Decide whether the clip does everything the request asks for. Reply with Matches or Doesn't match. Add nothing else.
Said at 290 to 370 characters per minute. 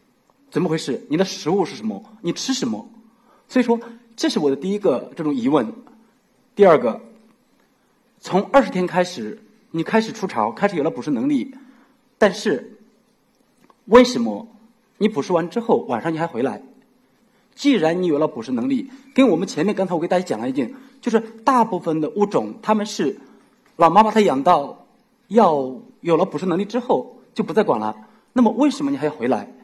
Doesn't match